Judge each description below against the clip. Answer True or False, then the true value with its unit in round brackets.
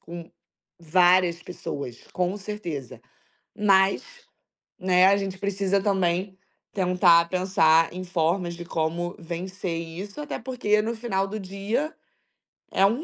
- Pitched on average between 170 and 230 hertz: True (185 Hz)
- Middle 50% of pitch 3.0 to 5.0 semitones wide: False (2.5 semitones)